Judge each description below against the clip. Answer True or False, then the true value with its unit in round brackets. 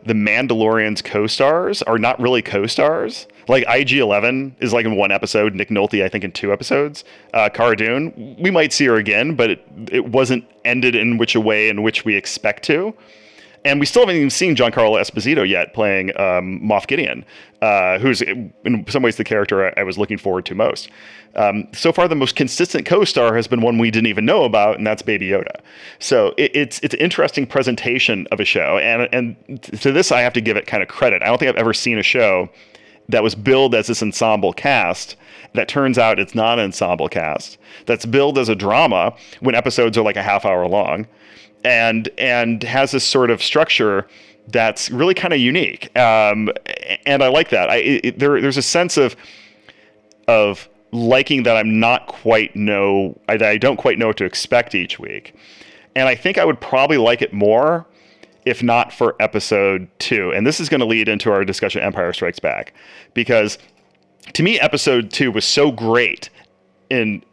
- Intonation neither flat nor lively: True (3.9 semitones)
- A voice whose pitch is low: True (115 Hz)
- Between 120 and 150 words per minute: False (200 wpm)